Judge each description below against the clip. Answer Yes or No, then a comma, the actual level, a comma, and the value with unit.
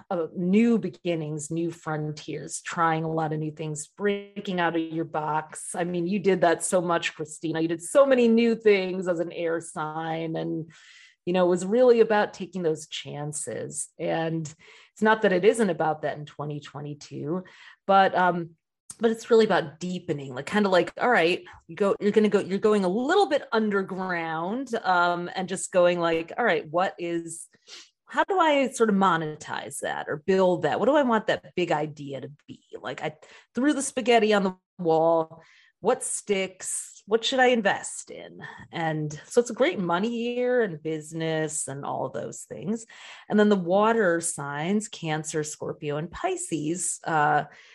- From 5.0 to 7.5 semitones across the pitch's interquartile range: No, average, 4.6 semitones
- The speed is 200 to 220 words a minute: No, average, 185 wpm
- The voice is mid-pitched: Yes, medium, 175 Hz